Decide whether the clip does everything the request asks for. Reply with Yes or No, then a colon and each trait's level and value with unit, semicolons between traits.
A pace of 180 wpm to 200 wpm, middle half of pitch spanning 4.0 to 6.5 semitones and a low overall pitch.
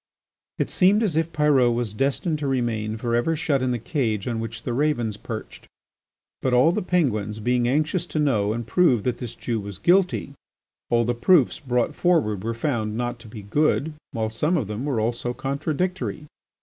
Yes: average, 190 wpm; average, 5.1 semitones; low, 125 Hz